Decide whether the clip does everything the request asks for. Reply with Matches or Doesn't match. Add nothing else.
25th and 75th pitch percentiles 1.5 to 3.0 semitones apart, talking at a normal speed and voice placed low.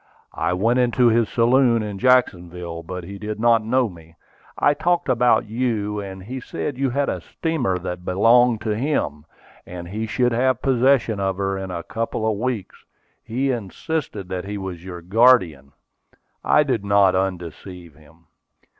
Doesn't match